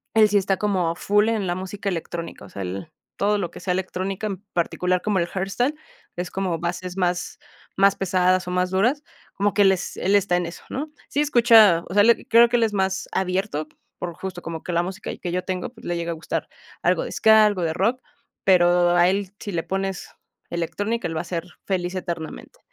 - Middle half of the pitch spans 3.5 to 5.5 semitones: No, average, 2.7 semitones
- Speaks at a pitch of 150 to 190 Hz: Yes, medium, 185 Hz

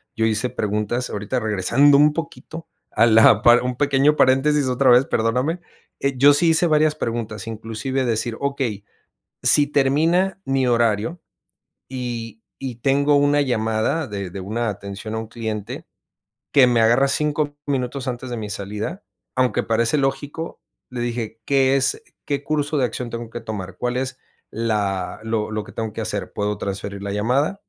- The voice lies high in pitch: No, low, 125 Hz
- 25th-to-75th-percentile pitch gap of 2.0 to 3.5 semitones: No, average, 4.2 semitones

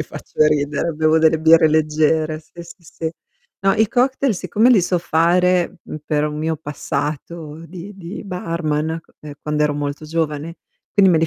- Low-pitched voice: No, medium, 160 Hz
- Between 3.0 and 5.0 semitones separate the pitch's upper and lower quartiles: No, narrow, 2.4 semitones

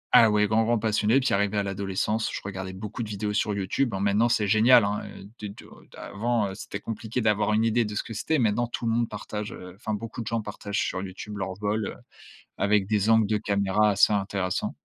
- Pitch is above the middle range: No, low, 105 Hz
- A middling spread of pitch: No, narrow, 1.9 semitones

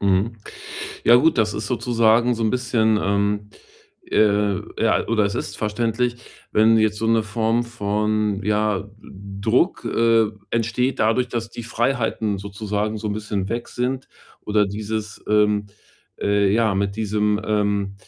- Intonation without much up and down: Yes, narrow, 2.0 semitones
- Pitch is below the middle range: Yes, low, 110 Hz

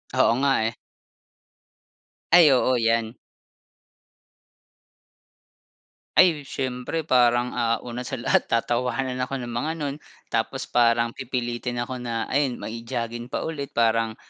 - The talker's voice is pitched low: Yes, low, 120 Hz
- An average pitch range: No, narrow, 2.1 semitones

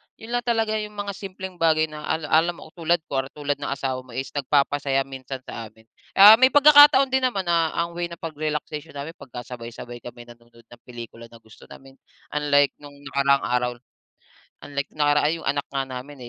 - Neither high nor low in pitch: Yes, medium, 145 Hz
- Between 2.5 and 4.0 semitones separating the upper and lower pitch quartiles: No, average, 4.6 semitones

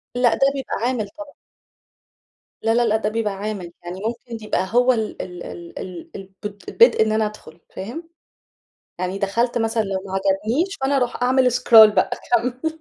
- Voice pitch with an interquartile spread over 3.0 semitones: Yes, average, 4.0 semitones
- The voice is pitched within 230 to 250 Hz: No, high, 220 Hz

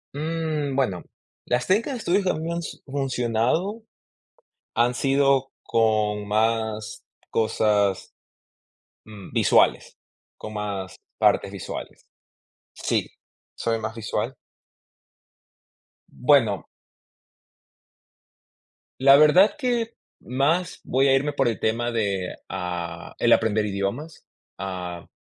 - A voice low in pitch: Yes, low, 120 Hz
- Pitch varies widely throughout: Yes, wide, 5.9 semitones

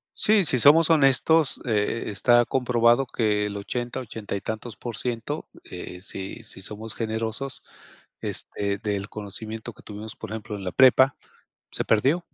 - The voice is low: Yes, low, 115 Hz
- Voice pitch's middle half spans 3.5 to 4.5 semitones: Yes, average, 3.9 semitones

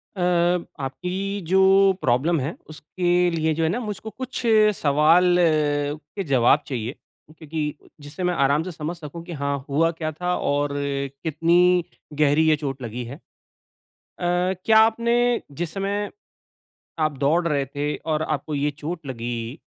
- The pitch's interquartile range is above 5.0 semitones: No, average, 3.8 semitones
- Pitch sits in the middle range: Yes, medium, 155 Hz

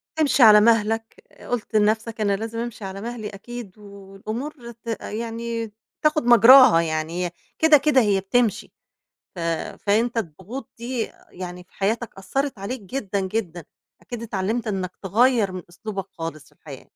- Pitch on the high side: Yes, high, 220 Hz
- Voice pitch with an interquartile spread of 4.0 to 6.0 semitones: No, average, 3.6 semitones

